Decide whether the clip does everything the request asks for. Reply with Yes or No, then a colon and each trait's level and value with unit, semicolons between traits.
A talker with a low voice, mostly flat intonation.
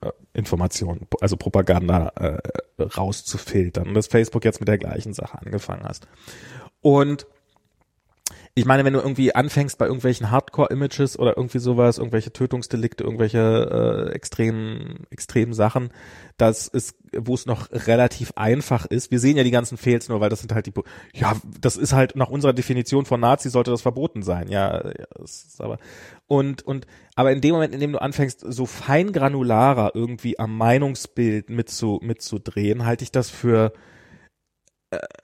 No: low, 120 Hz; average, 3.3 semitones